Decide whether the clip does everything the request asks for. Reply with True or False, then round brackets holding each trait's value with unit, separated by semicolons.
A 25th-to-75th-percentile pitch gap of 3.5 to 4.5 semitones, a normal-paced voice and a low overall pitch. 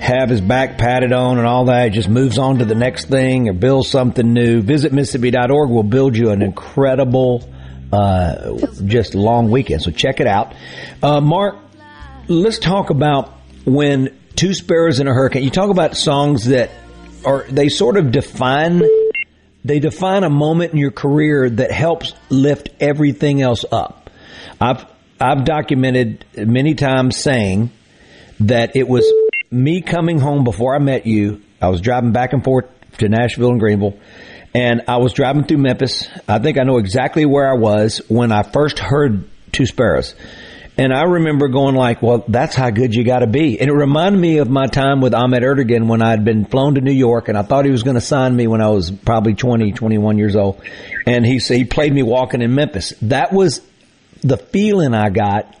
True (4.0 semitones; 190 wpm; 130 Hz)